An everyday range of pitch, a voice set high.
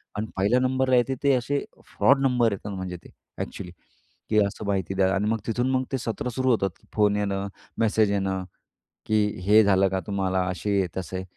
No: average, 4.1 semitones; low, 100 Hz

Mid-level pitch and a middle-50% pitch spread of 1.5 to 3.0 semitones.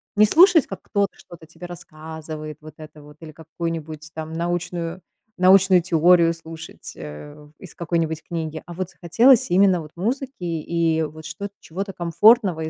Yes: medium, 165 Hz; average, 2.7 semitones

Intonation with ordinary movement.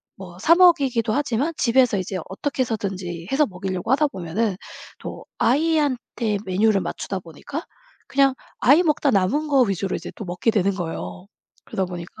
No: wide, 6.8 semitones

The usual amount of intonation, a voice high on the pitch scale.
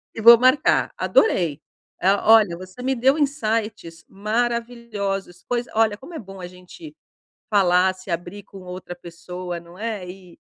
Yes: average, 4.6 semitones; high, 200 Hz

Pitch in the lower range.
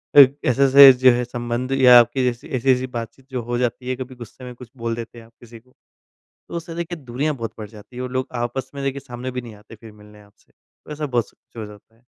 Yes: low, 125 Hz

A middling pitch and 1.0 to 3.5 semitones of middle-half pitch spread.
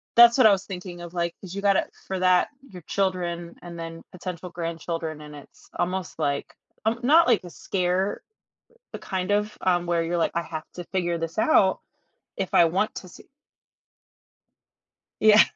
Yes: medium, 180 Hz; narrow, 2.5 semitones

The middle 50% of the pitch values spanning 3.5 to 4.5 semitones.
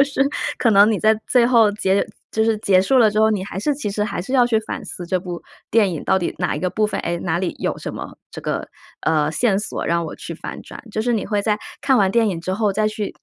No: average, 3.1 semitones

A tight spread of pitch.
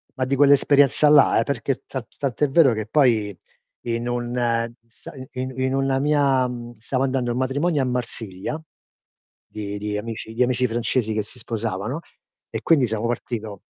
No: average, 3.1 semitones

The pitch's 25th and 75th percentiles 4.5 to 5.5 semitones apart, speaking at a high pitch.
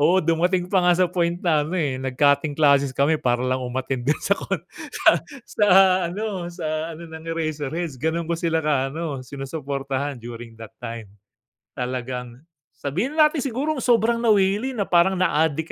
No: average, 4.8 semitones; medium, 155 Hz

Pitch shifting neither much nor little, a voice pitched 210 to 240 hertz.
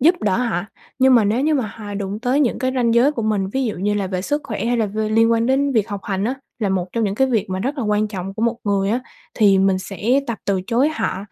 Yes: average, 3.8 semitones; high, 220 Hz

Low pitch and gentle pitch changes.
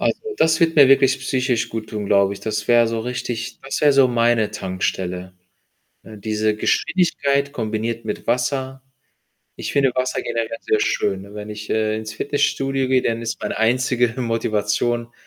No: low, 115 Hz; average, 3.6 semitones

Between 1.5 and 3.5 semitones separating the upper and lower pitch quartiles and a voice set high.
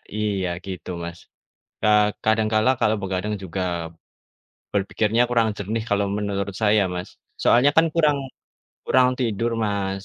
No: narrow, 2.5 semitones; low, 105 Hz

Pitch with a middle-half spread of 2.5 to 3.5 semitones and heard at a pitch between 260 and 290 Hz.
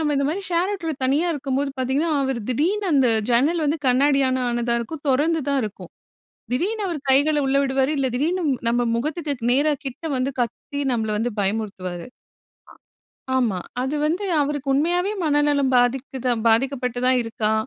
No: average, 3.9 semitones; very high, 275 Hz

